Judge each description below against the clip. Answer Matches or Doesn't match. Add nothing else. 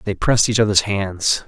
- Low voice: Matches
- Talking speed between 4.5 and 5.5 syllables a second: Matches